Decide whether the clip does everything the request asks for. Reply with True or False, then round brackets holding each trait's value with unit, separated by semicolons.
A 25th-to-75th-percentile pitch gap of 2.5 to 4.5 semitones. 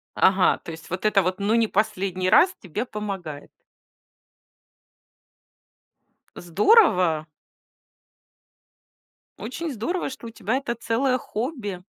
False (4.9 semitones)